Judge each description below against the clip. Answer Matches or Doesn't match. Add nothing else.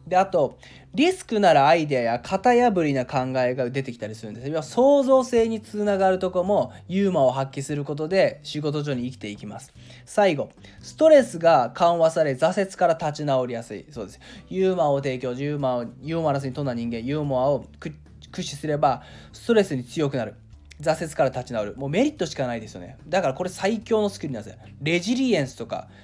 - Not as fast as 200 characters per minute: Doesn't match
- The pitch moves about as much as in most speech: Doesn't match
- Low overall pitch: Doesn't match